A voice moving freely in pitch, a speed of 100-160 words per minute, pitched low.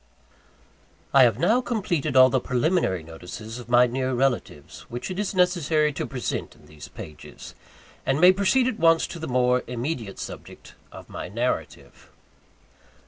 Yes: wide, 6.0 semitones; average, 155 wpm; low, 130 Hz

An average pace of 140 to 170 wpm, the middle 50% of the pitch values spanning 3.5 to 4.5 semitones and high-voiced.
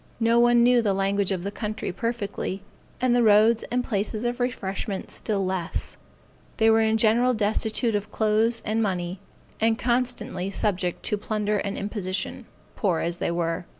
No: average, 165 wpm; average, 2.9 semitones; high, 215 Hz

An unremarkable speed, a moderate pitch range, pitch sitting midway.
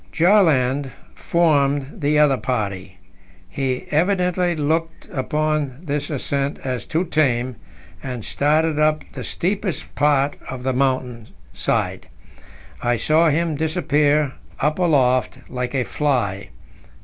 No: slow, 115 wpm; average, 3.5 semitones; medium, 145 Hz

